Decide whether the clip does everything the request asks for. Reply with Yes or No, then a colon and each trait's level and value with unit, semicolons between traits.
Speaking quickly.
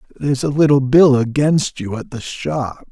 No: average, 185 wpm